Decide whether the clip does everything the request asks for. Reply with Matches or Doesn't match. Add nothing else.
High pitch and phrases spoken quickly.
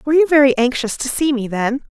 Matches